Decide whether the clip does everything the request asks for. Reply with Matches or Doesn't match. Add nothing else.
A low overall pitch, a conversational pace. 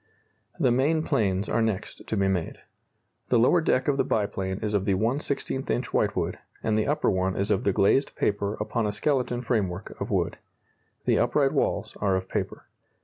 Matches